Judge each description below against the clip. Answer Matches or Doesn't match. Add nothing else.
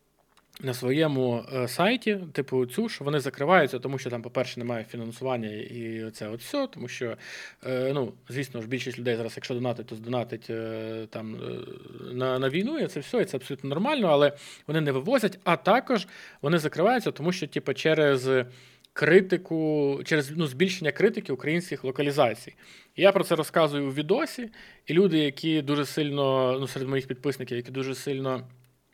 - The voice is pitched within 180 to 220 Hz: Doesn't match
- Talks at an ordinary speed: Doesn't match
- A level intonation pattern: Doesn't match